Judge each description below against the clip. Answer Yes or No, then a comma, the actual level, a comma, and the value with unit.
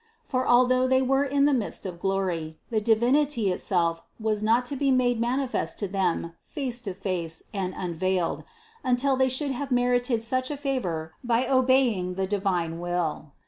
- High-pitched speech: Yes, high, 230 Hz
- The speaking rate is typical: Yes, average, 170 wpm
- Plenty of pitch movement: Yes, wide, 5.8 semitones